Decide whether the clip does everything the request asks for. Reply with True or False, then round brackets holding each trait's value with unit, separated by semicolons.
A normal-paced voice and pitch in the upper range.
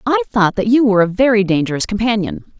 False (210 wpm; 215 Hz)